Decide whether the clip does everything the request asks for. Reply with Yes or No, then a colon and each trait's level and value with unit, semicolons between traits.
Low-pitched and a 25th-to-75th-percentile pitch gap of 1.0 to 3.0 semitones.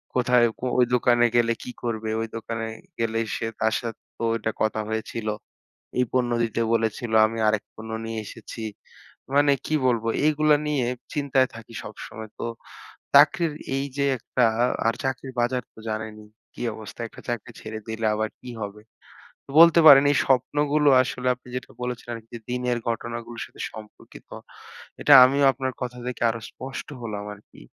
Yes: low, 120 Hz; narrow, 2.6 semitones